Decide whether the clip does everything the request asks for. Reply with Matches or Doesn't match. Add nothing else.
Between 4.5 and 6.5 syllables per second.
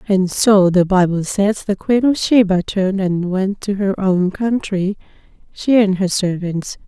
Doesn't match